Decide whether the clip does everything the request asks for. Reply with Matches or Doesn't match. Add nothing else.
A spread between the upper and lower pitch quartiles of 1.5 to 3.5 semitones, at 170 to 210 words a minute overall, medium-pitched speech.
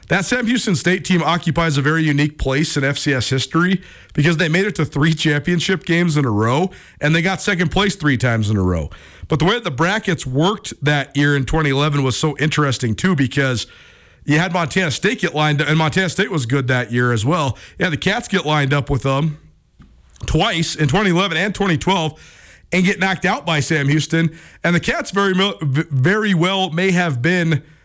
Doesn't match